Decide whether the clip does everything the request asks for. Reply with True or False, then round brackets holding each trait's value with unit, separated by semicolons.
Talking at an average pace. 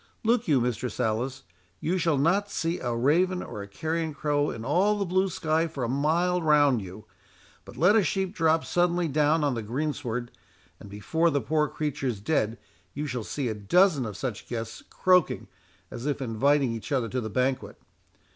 True (190 wpm)